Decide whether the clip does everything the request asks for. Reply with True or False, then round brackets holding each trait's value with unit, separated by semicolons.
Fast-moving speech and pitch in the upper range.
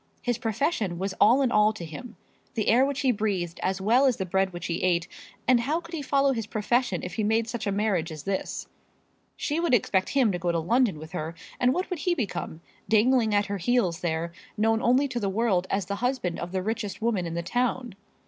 True (235 wpm; 215 Hz)